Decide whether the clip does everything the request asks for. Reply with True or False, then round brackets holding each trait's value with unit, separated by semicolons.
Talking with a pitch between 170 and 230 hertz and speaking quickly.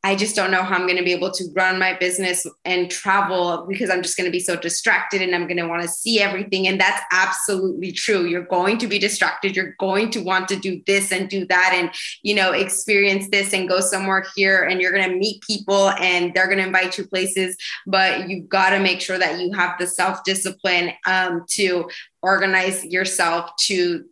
True (185 Hz; 210 wpm)